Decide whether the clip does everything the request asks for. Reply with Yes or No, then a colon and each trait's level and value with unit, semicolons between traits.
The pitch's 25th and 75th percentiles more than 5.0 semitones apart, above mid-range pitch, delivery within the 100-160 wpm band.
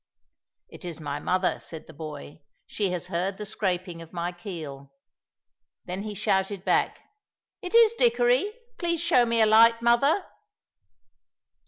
Yes: wide, 5.6 semitones; high, 195 Hz; average, 145 wpm